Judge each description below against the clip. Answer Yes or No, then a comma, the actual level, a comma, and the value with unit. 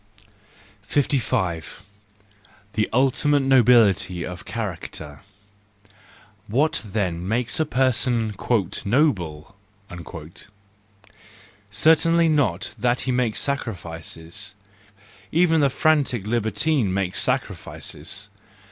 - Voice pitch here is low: Yes, low, 110 Hz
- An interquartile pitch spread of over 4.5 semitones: Yes, wide, 5.4 semitones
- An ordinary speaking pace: No, slow, 80 wpm